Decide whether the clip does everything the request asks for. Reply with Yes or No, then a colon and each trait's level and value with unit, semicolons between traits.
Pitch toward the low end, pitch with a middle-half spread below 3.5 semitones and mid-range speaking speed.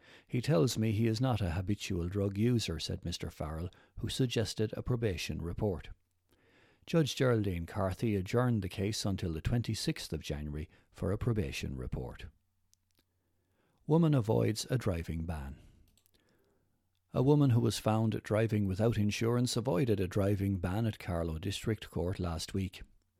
No: low, 100 Hz; average, 4.2 semitones; average, 145 wpm